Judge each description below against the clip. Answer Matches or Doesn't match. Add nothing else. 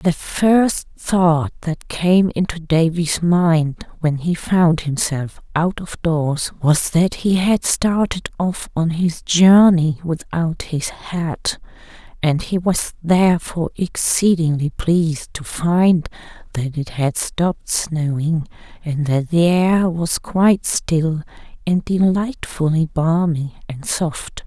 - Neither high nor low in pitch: Matches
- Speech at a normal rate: Doesn't match